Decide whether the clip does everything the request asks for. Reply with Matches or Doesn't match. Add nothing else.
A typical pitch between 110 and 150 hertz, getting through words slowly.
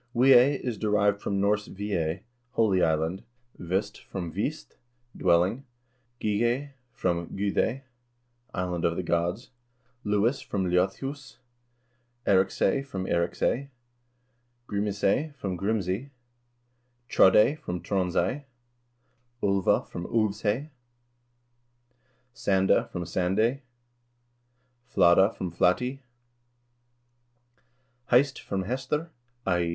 Doesn't match